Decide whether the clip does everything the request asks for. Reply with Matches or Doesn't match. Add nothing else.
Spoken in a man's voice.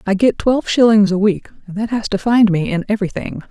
Doesn't match